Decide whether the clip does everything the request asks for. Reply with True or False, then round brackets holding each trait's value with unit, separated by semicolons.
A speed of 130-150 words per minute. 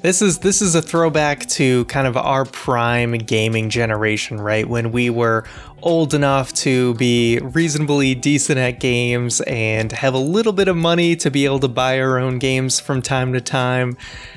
False (185 wpm)